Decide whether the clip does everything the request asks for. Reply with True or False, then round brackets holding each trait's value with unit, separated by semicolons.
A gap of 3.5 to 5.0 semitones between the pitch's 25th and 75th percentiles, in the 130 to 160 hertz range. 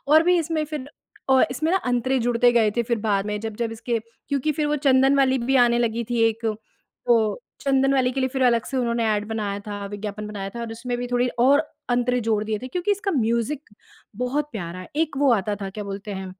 False (3.8 semitones; 240 Hz)